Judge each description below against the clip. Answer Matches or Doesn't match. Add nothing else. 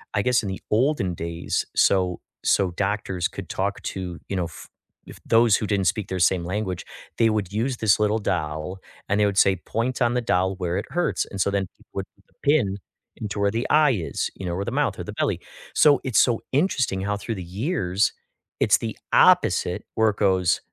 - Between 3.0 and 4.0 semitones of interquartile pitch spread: Matches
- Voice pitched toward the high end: Doesn't match